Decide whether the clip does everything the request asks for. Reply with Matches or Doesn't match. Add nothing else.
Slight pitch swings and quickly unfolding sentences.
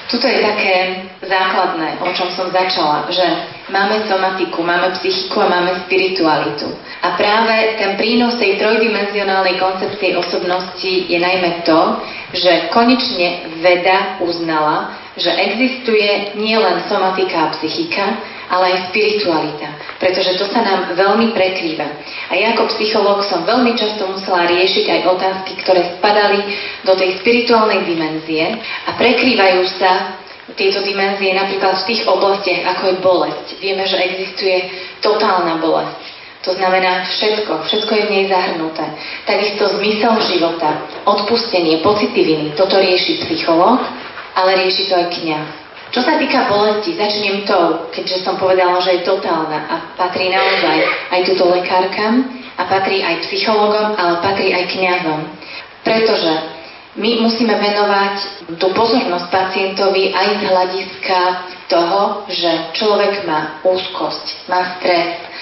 Doesn't match